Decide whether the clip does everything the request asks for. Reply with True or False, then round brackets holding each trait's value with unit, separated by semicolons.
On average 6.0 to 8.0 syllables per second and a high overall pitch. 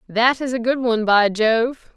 False (4.5 syllables/s; 235 Hz)